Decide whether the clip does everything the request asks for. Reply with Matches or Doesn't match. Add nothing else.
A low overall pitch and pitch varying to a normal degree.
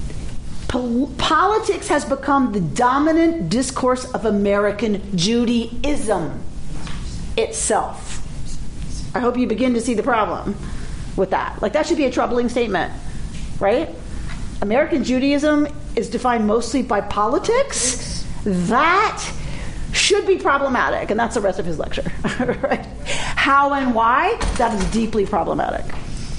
Doesn't match